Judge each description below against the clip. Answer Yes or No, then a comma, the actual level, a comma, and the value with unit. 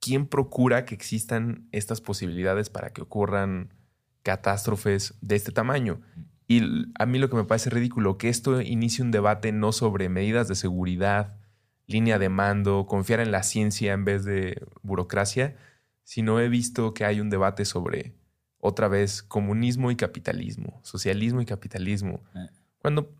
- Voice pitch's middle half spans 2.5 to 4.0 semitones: Yes, average, 3.2 semitones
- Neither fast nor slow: Yes, average, 155 wpm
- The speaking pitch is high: No, low, 110 Hz